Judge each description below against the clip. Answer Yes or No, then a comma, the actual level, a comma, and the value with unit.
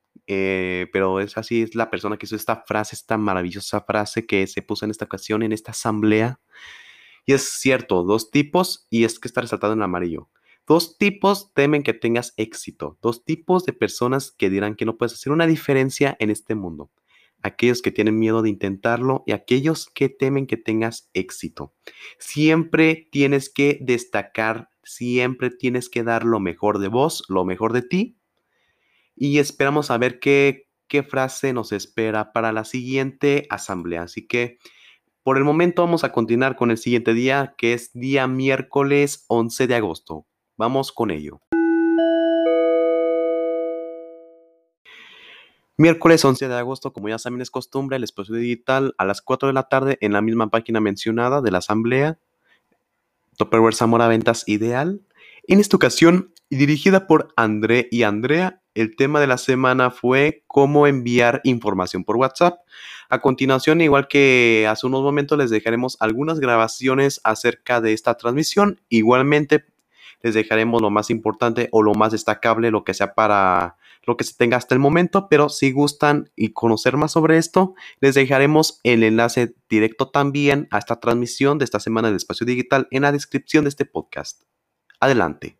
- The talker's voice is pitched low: Yes, low, 125 Hz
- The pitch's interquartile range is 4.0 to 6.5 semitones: Yes, average, 4.4 semitones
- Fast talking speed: No, average, 165 wpm